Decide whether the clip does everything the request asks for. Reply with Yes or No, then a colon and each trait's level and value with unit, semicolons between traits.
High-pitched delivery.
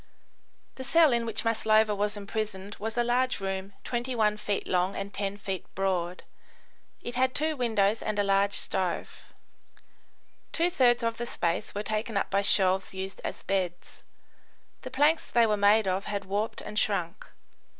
Yes: high, 210 Hz